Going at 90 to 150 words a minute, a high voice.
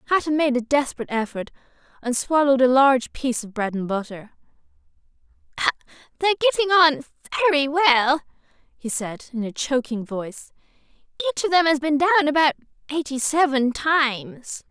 Yes: average, 145 wpm; very high, 275 Hz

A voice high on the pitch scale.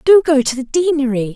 Yes: very high, 280 Hz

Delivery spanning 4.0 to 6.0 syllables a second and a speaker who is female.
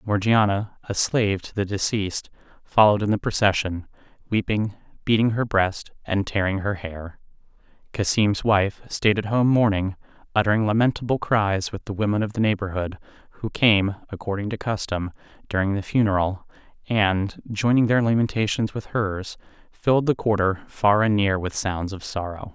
No: 5.0 syllables/s; male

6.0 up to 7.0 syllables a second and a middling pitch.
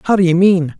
Yes: 6.5 syllables/s; medium, 175 Hz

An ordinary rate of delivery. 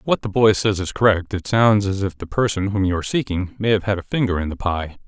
No: fast, 295 wpm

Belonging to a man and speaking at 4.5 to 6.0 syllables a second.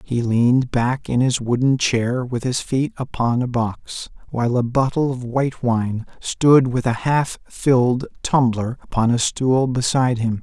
No: male; 4.2 syllables/s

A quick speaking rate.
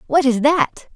No: average, 190 wpm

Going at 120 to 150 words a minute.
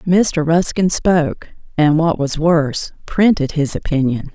Yes: average, 140 wpm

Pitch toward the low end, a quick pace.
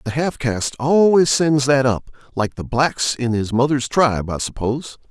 No: low, 130 Hz; average, 175 wpm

